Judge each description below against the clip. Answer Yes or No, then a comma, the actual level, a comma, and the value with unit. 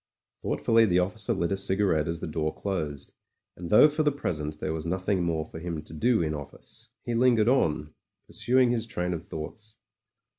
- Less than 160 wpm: No, average, 190 wpm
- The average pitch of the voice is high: No, very low, 90 Hz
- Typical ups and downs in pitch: No, wide, 6.2 semitones